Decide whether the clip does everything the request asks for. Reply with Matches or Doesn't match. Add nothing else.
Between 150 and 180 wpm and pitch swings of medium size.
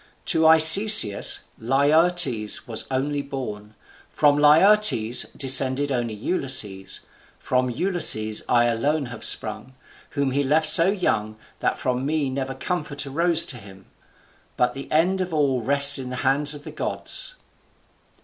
Doesn't match